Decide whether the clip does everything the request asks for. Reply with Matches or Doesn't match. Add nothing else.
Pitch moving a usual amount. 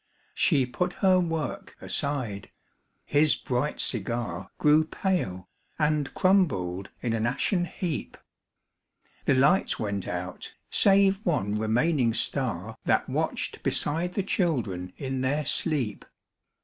Doesn't match